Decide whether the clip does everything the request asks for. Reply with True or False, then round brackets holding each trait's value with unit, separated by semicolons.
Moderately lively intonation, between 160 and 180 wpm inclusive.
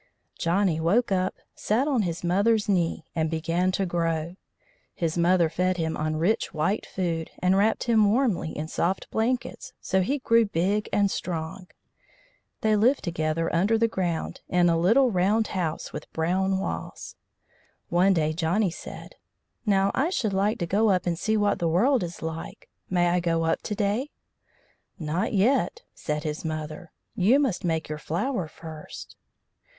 True (4.2 semitones; 165 wpm)